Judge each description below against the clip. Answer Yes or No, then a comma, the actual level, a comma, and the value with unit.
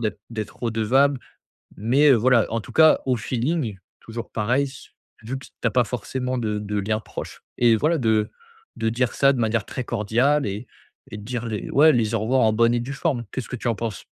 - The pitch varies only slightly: No, average, 3.0 semitones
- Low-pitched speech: Yes, low, 120 Hz